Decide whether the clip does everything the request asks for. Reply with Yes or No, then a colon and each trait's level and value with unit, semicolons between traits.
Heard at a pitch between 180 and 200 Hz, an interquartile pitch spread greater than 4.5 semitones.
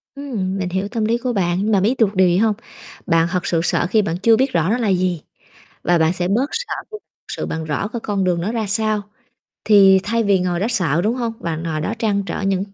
No: high, 195 Hz; average, 4.0 semitones